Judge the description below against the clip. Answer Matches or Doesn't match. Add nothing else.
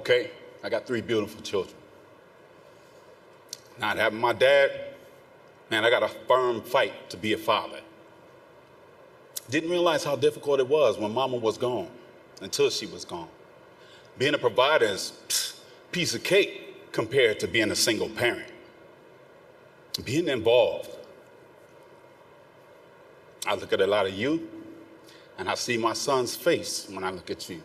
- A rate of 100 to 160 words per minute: Matches